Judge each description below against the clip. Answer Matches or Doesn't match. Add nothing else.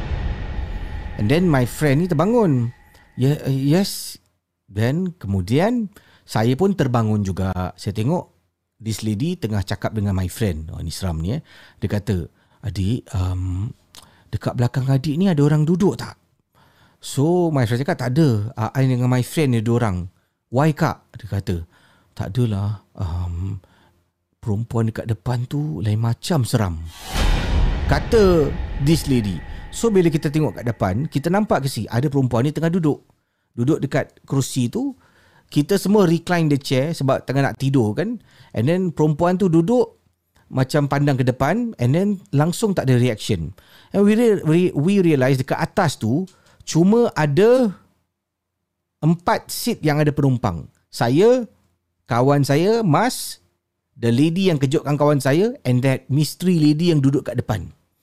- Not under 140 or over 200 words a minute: Matches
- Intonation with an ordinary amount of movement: Doesn't match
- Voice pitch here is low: Matches